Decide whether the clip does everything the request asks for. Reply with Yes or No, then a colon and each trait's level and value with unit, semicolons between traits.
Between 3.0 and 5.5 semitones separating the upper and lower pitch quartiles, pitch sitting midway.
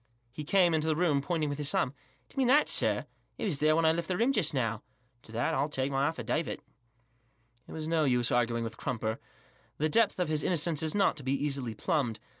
Yes: average, 4.2 semitones; medium, 150 Hz